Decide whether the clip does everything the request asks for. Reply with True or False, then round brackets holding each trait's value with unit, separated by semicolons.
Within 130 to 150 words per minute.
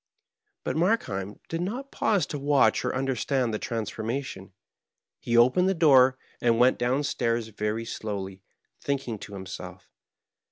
True (145 wpm)